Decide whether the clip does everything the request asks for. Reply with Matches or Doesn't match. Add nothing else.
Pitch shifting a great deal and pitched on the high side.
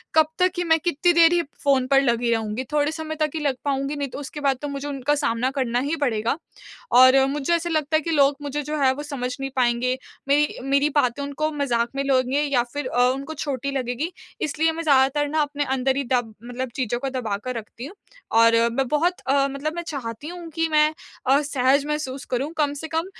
Doesn't match